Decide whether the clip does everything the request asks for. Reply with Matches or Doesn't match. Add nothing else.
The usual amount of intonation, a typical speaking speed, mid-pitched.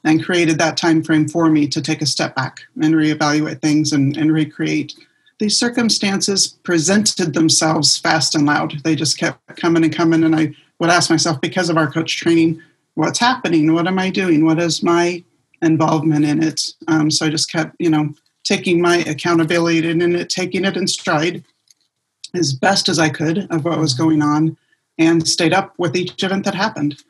Doesn't match